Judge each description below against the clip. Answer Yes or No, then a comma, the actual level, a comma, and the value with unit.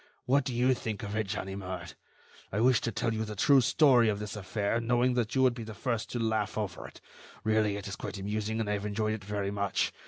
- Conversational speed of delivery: No, fast, 245 wpm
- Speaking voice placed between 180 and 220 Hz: No, low, 110 Hz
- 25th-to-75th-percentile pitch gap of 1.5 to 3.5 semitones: Yes, average, 2.7 semitones